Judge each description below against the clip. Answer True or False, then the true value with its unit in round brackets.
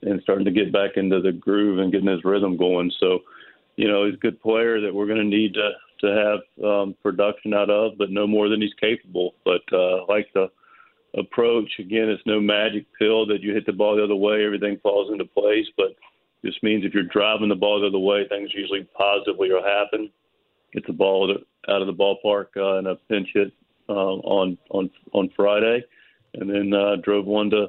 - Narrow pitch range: True (1.4 semitones)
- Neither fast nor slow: False (215 wpm)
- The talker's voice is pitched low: True (105 Hz)